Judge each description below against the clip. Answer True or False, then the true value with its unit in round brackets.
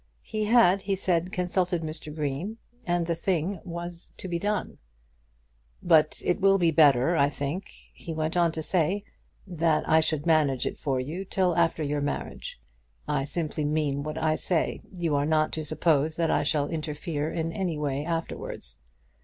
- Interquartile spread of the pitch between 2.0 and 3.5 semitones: True (2.8 semitones)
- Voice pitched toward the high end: False (160 Hz)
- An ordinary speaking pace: True (175 wpm)